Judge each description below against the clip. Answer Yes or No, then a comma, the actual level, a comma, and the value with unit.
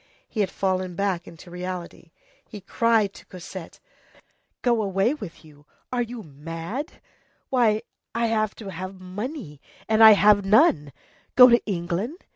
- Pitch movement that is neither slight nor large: Yes, average, 4.3 semitones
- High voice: Yes, high, 200 Hz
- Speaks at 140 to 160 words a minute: Yes, average, 150 wpm